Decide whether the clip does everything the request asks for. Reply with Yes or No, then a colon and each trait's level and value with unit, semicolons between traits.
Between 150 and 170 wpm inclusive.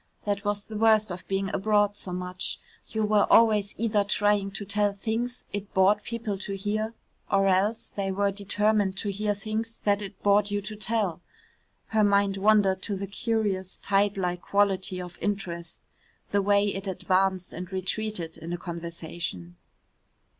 Yes: average, 165 wpm